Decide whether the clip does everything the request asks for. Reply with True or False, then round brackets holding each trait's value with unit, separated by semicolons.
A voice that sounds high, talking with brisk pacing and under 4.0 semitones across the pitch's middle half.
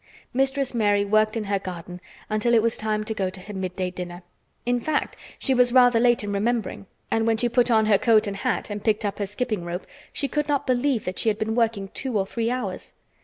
True (220 Hz; 235 wpm; 3.3 semitones)